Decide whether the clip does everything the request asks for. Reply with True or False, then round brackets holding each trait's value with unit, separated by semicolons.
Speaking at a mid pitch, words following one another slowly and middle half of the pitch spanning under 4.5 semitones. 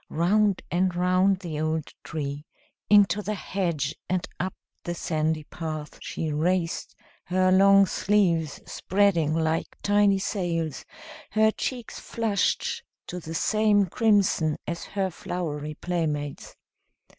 True (180 Hz; 120 wpm; 3.8 semitones)